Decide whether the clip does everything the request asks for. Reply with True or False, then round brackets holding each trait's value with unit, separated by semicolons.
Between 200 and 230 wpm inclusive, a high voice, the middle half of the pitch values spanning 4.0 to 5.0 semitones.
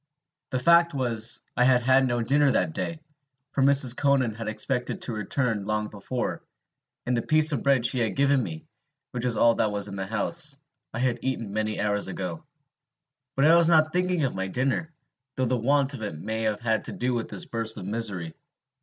False (205 wpm; 125 Hz; 4.3 semitones)